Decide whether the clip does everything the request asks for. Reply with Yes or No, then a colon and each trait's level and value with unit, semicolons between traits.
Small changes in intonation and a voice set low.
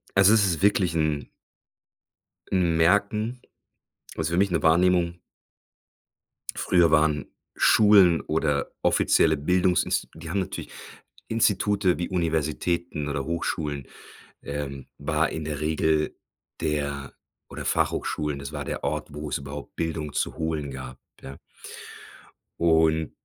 No: average, 3.1 semitones; very low, 80 Hz